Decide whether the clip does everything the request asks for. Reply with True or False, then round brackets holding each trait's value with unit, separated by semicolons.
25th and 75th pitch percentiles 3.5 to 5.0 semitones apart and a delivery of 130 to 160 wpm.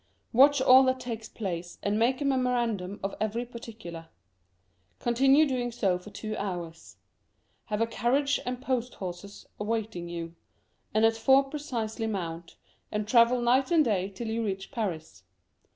True (4.2 semitones; 150 wpm)